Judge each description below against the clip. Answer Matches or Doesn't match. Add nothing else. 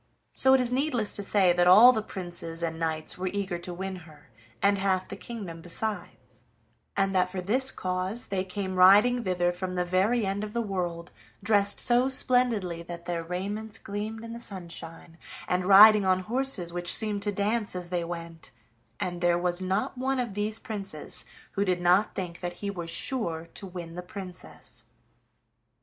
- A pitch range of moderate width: Matches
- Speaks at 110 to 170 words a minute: Doesn't match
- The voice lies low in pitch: Doesn't match